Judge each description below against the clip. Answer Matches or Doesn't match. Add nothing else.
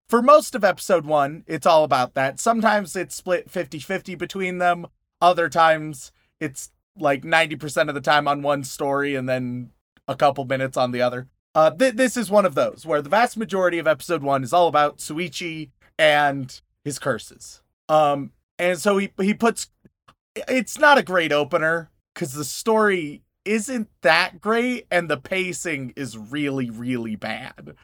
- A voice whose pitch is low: Doesn't match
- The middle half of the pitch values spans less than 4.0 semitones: Doesn't match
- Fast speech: Doesn't match